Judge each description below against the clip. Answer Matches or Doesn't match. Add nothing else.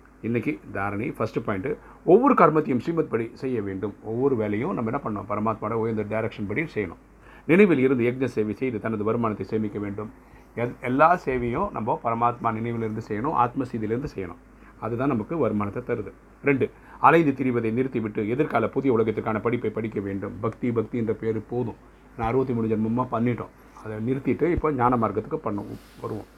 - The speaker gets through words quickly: Matches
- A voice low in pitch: Matches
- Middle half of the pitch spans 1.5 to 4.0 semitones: Matches